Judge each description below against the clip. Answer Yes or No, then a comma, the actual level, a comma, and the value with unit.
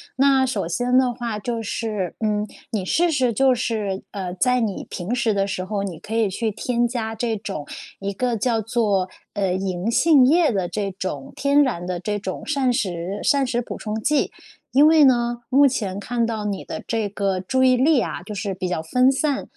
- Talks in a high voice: Yes, high, 225 Hz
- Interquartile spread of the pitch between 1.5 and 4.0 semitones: No, average, 4.4 semitones